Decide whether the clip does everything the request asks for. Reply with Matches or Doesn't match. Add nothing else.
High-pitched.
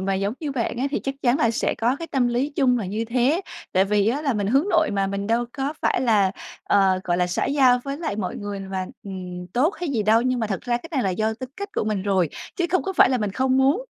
Matches